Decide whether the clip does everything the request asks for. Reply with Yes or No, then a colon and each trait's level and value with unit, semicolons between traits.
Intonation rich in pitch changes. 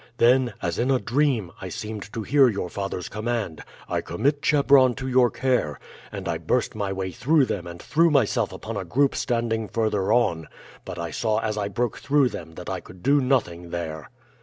Yes: wide, 6.2 semitones